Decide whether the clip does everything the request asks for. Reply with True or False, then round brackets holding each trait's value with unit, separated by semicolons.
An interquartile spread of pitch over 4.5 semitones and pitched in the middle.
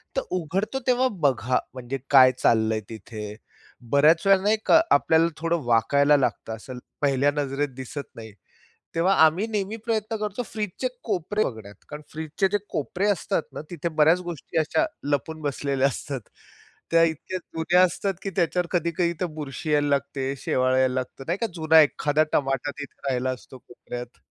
True (5.4 semitones; 150 Hz)